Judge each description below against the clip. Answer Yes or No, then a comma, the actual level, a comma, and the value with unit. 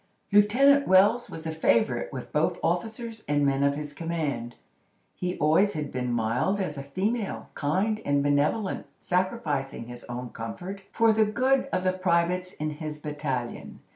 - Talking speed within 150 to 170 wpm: Yes, average, 155 wpm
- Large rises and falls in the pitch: Yes, wide, 6.4 semitones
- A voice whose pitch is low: No, medium, 170 Hz